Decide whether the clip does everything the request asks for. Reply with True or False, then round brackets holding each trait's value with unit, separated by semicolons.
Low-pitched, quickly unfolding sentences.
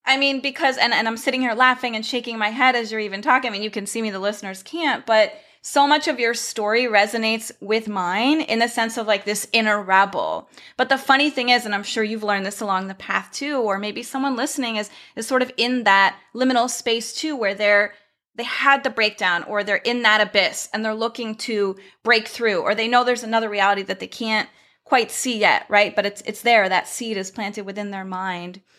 False (225 Hz; 235 wpm)